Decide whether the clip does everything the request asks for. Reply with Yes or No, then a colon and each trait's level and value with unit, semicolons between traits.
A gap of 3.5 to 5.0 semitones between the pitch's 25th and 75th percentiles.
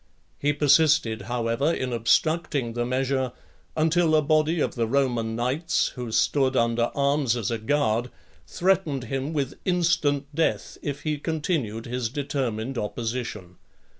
Yes: average, 4.5 semitones